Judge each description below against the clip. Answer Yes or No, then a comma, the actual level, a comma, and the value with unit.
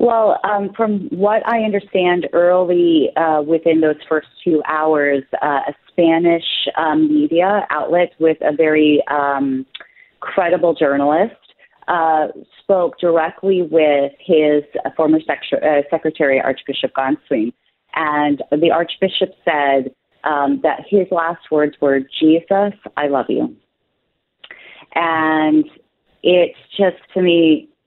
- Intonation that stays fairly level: No, average, 3.2 semitones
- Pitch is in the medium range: Yes, medium, 160 Hz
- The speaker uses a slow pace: Yes, slow, 120 wpm